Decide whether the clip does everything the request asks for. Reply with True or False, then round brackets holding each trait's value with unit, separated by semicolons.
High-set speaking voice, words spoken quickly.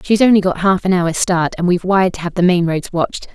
False (180 Hz; 285 wpm)